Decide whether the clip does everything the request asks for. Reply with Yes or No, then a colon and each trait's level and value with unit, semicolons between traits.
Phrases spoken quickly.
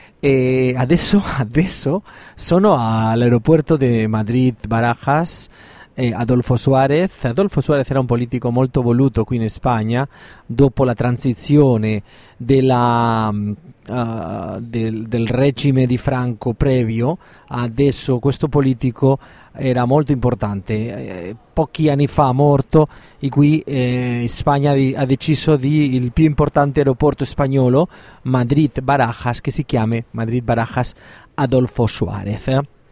No: average, 120 wpm